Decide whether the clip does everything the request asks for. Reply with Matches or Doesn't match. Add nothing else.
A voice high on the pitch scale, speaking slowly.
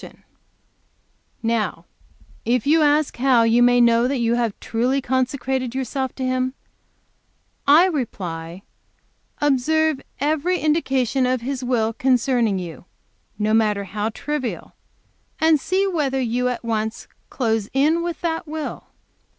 Matches